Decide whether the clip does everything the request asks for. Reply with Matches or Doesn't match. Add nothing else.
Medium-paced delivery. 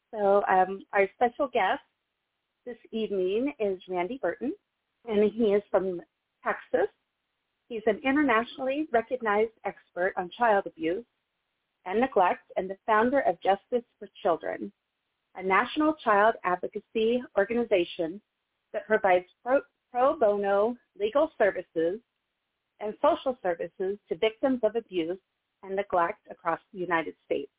Doesn't match